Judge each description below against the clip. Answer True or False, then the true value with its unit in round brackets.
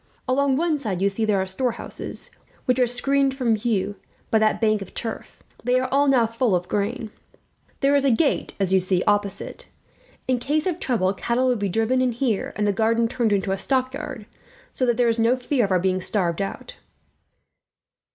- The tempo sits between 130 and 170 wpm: False (200 wpm)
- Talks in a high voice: True (230 Hz)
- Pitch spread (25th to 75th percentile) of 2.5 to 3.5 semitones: False (4.3 semitones)